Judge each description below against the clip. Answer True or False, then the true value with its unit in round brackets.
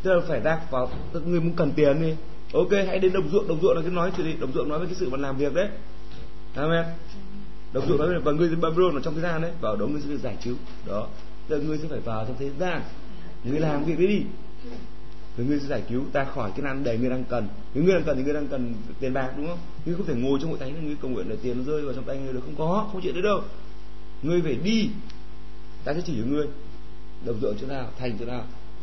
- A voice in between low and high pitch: True (150 Hz)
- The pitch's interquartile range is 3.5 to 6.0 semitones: True (5.1 semitones)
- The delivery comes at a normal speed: False (280 wpm)